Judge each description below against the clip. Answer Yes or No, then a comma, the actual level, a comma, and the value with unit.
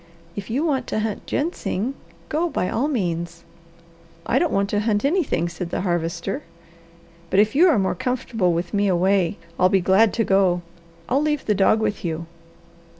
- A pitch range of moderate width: No, wide, 6.0 semitones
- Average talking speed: Yes, average, 180 wpm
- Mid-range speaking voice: No, high, 205 Hz